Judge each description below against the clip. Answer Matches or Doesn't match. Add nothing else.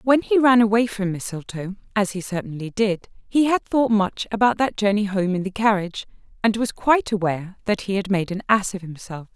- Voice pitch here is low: Doesn't match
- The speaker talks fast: Matches